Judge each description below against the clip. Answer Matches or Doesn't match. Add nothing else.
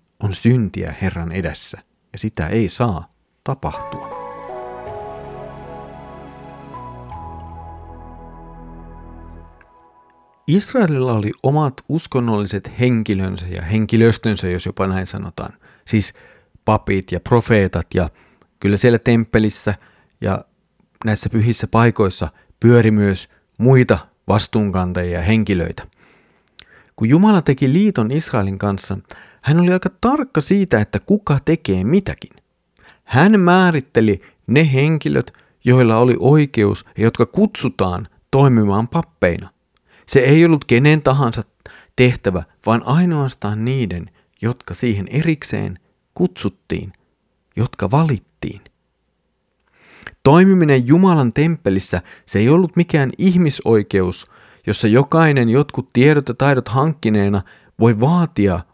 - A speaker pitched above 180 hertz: Doesn't match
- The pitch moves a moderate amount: Doesn't match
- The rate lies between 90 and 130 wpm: Matches